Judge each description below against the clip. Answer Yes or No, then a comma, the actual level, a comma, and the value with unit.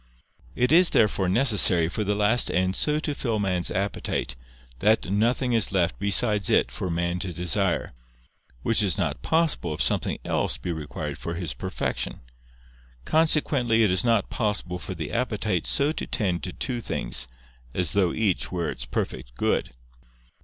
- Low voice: Yes, low, 100 Hz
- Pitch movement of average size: Yes, average, 4.7 semitones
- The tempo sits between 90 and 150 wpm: No, average, 165 wpm